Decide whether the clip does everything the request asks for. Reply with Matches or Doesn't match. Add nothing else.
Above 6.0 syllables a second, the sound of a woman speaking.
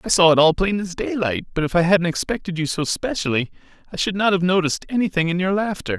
Doesn't match